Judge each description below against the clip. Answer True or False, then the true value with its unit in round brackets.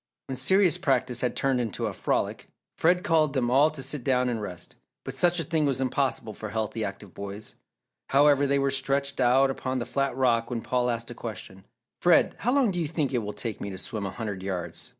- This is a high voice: False (130 Hz)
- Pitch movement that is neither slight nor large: True (4.0 semitones)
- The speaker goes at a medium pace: False (225 wpm)